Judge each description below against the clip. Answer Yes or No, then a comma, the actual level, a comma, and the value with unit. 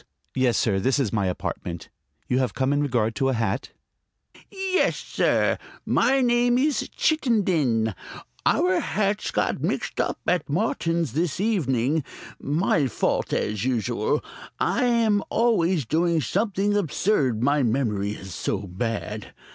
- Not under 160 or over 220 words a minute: No, slow, 135 wpm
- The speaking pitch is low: No, medium, 145 Hz